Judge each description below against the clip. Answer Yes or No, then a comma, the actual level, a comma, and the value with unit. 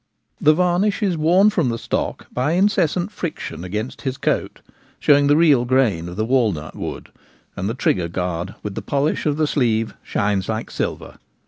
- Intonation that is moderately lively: No, wide, 7.4 semitones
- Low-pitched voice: Yes, low, 130 Hz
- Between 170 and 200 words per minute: Yes, average, 180 wpm